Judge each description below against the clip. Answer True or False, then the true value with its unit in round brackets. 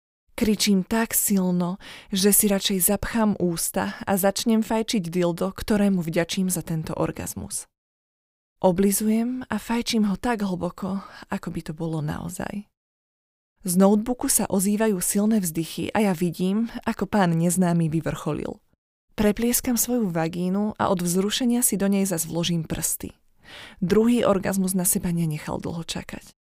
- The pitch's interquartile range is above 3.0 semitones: True (3.6 semitones)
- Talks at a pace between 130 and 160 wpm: True (135 wpm)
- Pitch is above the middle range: True (195 Hz)